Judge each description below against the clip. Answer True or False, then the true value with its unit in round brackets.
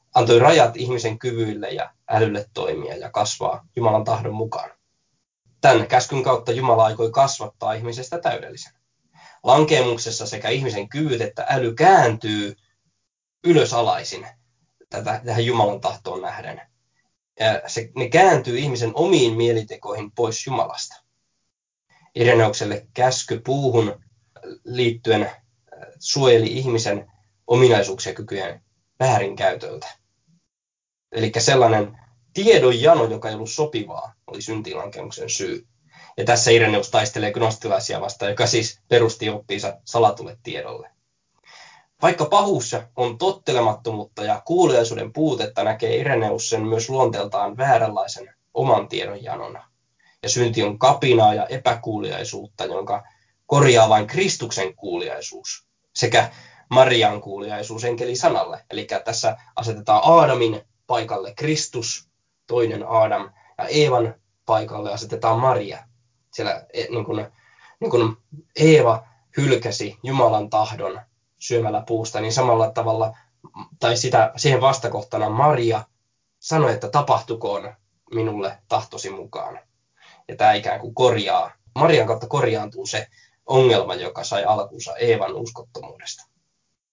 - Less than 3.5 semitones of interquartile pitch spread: True (2.7 semitones)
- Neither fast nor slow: True (105 wpm)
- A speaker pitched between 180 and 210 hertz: False (115 Hz)